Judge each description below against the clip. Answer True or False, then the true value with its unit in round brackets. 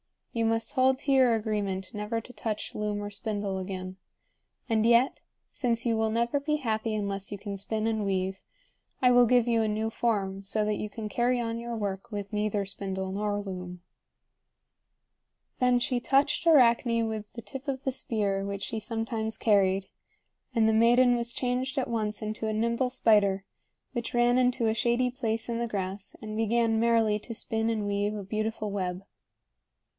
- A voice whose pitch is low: False (220 Hz)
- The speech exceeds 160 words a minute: True (180 wpm)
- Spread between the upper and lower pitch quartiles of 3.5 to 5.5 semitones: False (2.6 semitones)